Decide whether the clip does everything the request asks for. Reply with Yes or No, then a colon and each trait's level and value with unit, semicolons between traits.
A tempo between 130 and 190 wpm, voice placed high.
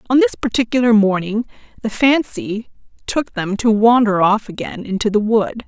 Yes: average, 160 wpm; high, 220 Hz